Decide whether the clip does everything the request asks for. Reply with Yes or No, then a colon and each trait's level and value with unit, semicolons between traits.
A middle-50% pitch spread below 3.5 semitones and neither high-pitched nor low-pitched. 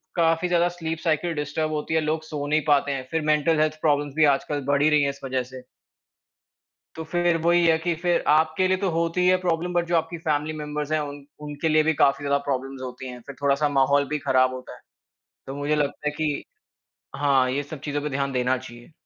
Yes: narrow, 2.5 semitones; medium, 150 Hz